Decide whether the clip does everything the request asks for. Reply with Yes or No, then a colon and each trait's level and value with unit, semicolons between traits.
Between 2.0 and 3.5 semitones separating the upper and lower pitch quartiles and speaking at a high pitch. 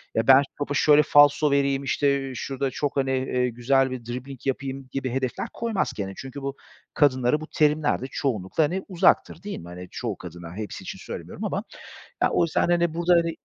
No: average, 2.9 semitones; low, 135 Hz